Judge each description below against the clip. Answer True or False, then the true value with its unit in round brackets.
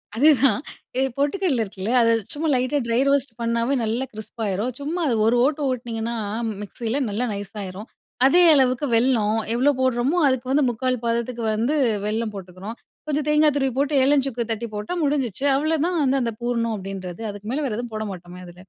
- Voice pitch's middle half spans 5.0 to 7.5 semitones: False (4.2 semitones)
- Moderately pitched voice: False (240 Hz)